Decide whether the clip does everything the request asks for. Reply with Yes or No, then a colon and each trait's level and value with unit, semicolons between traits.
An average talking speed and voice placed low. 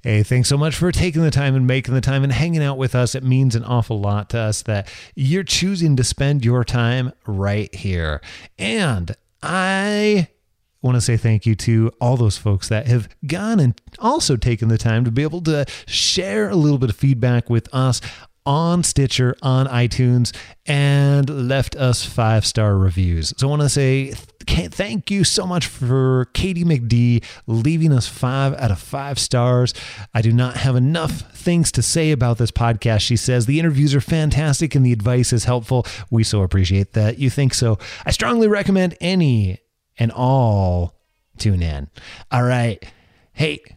Yes: average, 180 wpm; low, 125 Hz